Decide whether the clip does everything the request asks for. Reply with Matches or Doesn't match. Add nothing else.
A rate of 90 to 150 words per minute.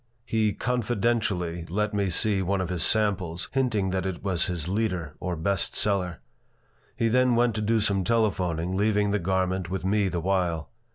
Doesn't match